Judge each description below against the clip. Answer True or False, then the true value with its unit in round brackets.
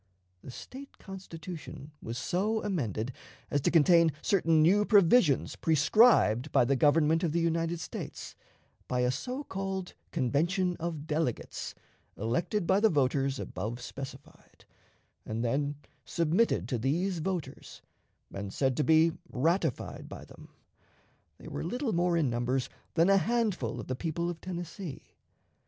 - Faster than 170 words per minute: False (140 wpm)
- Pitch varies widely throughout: True (5.7 semitones)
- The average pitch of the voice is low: False (165 Hz)